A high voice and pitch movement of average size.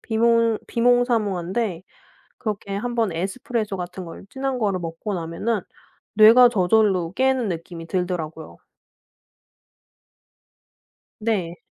Yes: high, 205 Hz; average, 4.7 semitones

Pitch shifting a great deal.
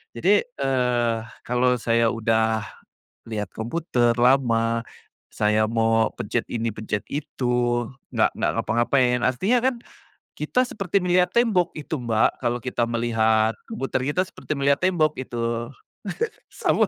No: average, 3.8 semitones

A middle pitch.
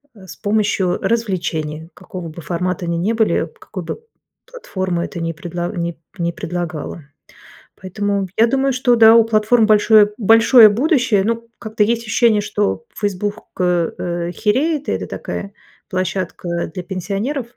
No: high, 205 Hz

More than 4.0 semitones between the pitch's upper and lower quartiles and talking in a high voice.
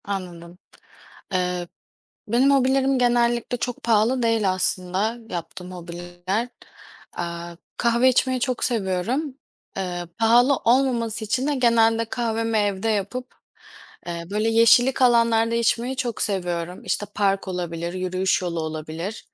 Yes: average, 4.9 semitones; high, 220 Hz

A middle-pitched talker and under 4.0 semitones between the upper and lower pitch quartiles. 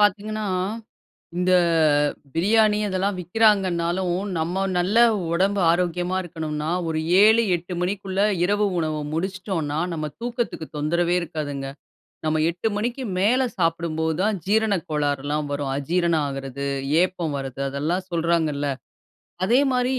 No: medium, 175 Hz; average, 4.4 semitones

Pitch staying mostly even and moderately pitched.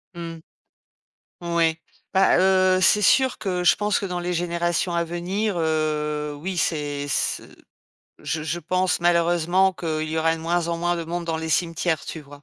Yes: narrow, 2.0 semitones; medium, 170 Hz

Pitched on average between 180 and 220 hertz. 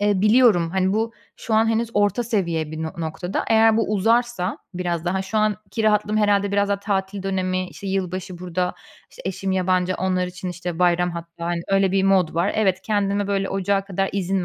Yes: high, 190 Hz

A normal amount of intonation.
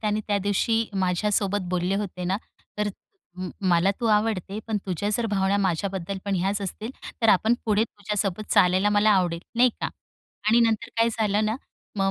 No: narrow, 2.3 semitones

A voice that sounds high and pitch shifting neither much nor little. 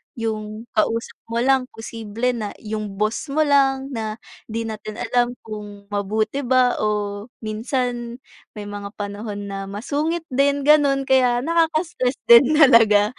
Yes: high, 230 Hz; average, 4.1 semitones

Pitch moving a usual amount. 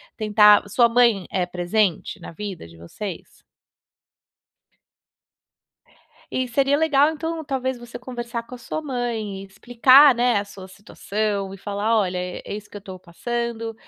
Yes: average, 3.9 semitones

